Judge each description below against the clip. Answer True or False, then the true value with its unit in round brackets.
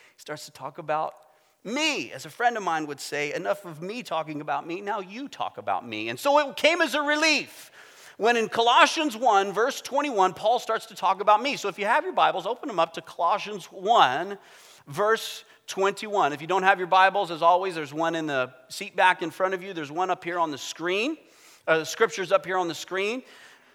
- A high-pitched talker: True (195 Hz)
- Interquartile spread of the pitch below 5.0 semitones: False (5.6 semitones)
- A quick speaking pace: True (225 wpm)